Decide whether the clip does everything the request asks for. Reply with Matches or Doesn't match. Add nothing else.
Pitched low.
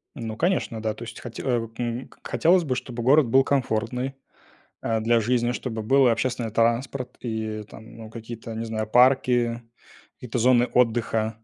Matches